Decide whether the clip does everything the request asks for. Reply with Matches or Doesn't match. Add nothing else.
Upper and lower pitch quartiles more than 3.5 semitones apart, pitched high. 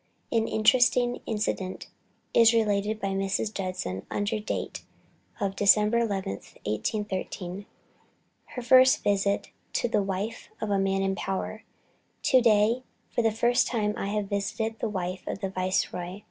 Doesn't match